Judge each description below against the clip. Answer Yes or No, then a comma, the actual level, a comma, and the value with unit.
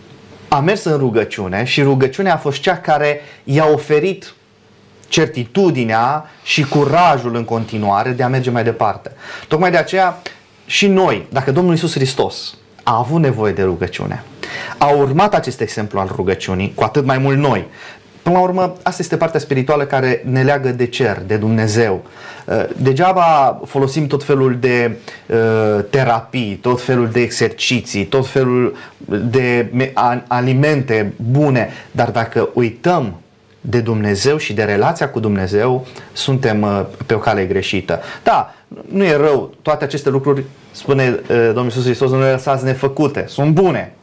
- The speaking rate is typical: Yes, average, 145 wpm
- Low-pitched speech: Yes, low, 130 Hz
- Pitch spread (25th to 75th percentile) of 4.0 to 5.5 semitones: Yes, average, 4.4 semitones